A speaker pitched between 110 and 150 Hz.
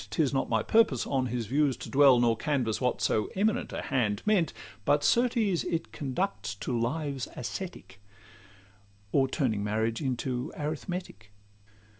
Yes: low, 135 Hz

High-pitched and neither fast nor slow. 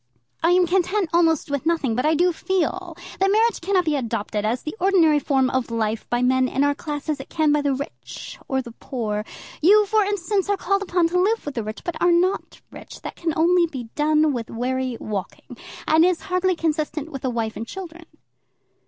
No: very high, 310 Hz; fast, 220 wpm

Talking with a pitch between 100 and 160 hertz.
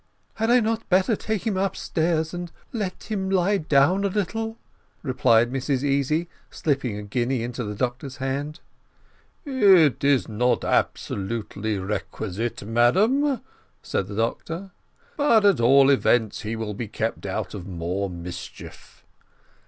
Yes: low, 135 Hz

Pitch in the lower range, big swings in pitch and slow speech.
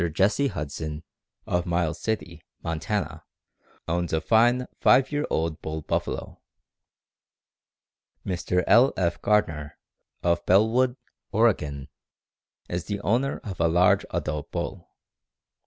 Yes: very low, 90 Hz; wide, 5.7 semitones; slow, 110 wpm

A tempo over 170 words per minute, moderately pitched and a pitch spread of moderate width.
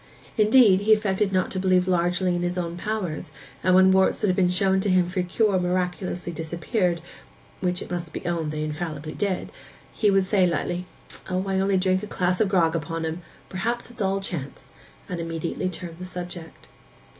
No: average, 180 wpm; medium, 180 Hz; narrow, 1.8 semitones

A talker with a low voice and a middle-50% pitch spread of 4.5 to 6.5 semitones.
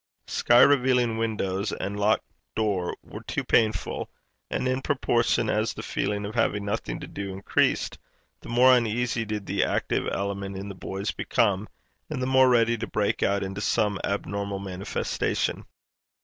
No: low, 105 Hz; average, 3.0 semitones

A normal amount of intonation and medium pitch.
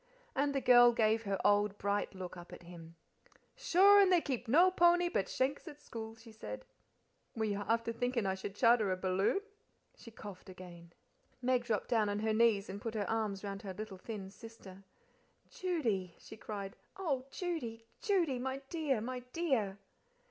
No: average, 4.8 semitones; high, 225 Hz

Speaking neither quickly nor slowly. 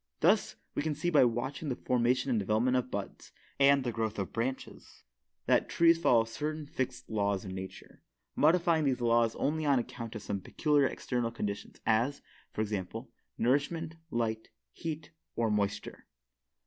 Yes: average, 160 wpm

